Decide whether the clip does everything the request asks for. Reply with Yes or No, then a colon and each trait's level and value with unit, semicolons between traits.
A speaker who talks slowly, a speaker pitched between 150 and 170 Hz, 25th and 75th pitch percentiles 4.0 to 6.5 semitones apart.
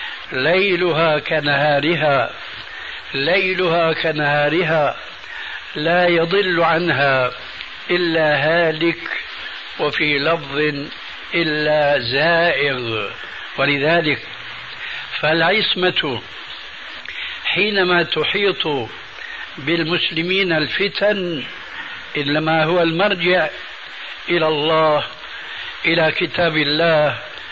No: slow, 60 wpm; medium, 165 Hz; average, 2.8 semitones